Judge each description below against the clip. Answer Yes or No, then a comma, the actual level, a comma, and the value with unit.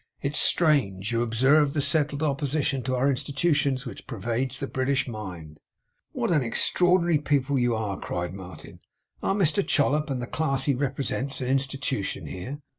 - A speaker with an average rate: Yes, average, 160 wpm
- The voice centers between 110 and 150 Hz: Yes, low, 135 Hz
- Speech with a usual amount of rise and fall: Yes, average, 3.5 semitones